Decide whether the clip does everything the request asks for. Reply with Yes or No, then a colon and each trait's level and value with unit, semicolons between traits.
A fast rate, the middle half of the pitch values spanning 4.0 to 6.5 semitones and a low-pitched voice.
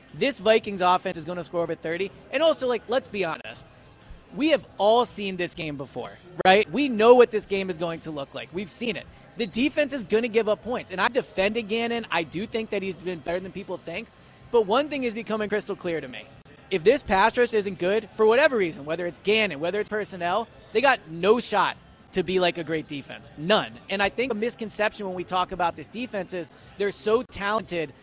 No: fast, 230 wpm; average, 4.4 semitones; high, 200 Hz